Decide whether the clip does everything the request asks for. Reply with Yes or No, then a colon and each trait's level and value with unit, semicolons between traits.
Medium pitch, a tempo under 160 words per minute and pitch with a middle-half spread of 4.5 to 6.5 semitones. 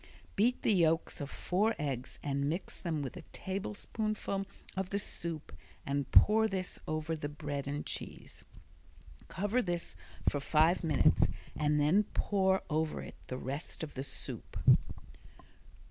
Yes: medium, 165 Hz; average, 145 wpm; average, 4.9 semitones